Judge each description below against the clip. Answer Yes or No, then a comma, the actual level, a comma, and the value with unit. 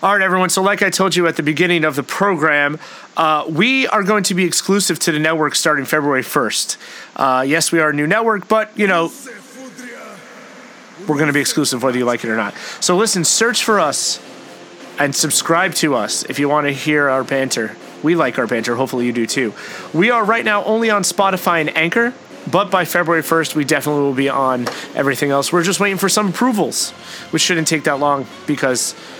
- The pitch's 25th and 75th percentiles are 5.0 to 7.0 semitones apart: Yes, wide, 5.6 semitones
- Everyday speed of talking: No, fast, 215 wpm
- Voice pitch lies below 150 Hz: No, medium, 160 Hz